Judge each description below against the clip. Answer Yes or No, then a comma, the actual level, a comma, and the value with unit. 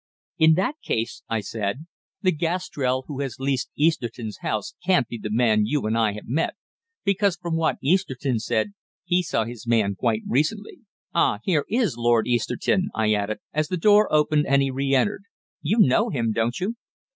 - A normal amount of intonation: No, wide, 7.0 semitones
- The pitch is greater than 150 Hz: No, low, 135 Hz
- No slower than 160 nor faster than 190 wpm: Yes, average, 180 wpm